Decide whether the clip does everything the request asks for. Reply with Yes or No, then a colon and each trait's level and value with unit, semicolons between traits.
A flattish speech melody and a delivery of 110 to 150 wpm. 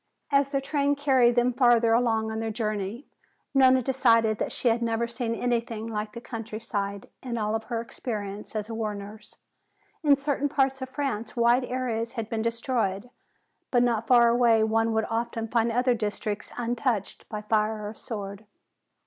No: narrow, 2.3 semitones; average, 170 wpm